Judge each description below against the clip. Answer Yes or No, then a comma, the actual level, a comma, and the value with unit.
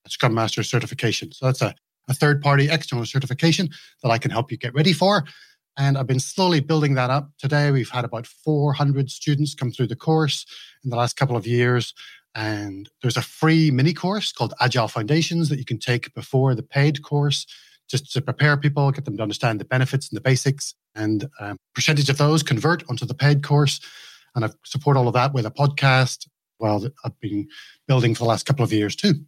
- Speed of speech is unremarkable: No, fast, 210 wpm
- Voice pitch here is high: No, low, 135 Hz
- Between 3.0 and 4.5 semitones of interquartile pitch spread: Yes, average, 3.3 semitones